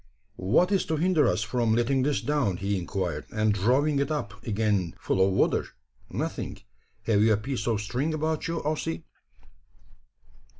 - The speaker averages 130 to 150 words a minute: No, average, 165 wpm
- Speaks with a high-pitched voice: No, low, 115 Hz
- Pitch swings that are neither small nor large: No, wide, 6.6 semitones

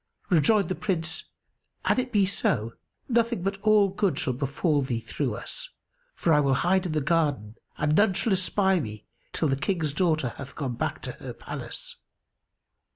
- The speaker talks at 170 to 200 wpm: Yes, average, 175 wpm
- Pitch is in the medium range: Yes, medium, 160 Hz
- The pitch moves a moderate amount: No, wide, 5.8 semitones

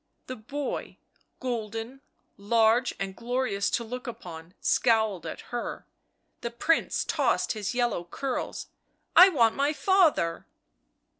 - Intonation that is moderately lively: Yes, average, 3.8 semitones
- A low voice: No, high, 235 Hz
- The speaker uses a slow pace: Yes, slow, 125 wpm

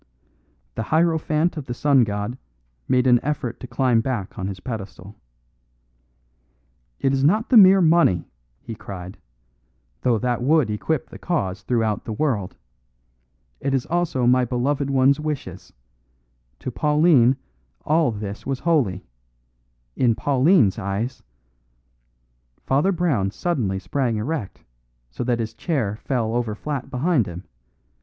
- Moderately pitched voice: No, low, 125 Hz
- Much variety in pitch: Yes, wide, 5.8 semitones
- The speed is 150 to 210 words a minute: No, slow, 135 wpm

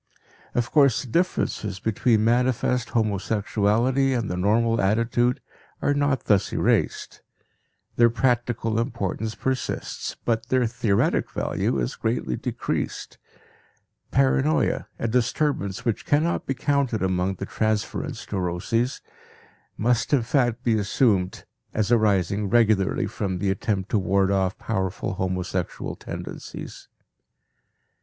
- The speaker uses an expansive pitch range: No, average, 3.8 semitones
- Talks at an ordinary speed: No, slow, 115 wpm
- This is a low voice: Yes, low, 110 Hz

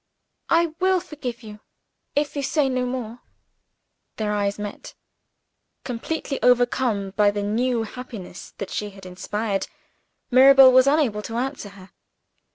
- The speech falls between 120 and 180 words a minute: Yes, slow, 135 wpm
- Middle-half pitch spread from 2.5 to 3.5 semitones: No, average, 4.4 semitones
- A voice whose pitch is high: Yes, high, 240 Hz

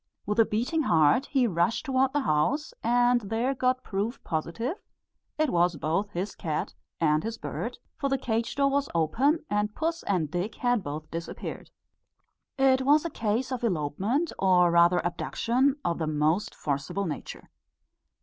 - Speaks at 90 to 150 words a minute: No, average, 160 wpm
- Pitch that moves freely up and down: Yes, wide, 7.4 semitones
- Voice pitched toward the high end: Yes, high, 220 Hz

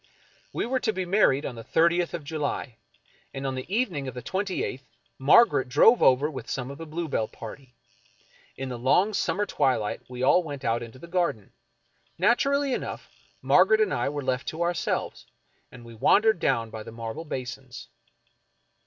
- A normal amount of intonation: No, wide, 6.2 semitones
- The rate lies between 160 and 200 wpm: Yes, average, 180 wpm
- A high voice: No, medium, 140 Hz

